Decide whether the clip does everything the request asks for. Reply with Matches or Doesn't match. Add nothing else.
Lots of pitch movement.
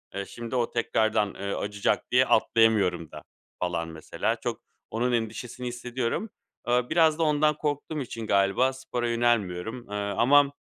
Doesn't match